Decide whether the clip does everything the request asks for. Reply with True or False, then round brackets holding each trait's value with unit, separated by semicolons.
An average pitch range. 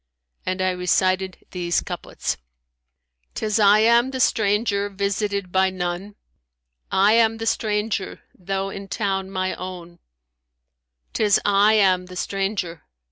False (2.1 semitones)